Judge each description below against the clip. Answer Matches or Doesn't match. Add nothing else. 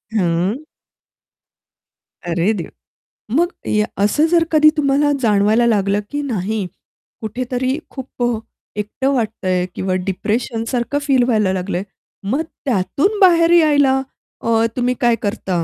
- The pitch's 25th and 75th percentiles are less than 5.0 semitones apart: Doesn't match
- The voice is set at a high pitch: Matches